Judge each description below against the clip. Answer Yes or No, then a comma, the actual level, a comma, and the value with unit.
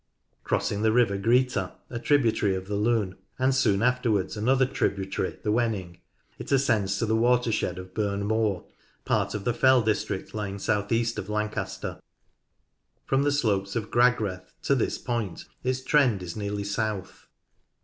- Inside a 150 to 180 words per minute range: Yes, average, 160 wpm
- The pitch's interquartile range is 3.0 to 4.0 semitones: Yes, average, 3.5 semitones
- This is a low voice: Yes, low, 110 Hz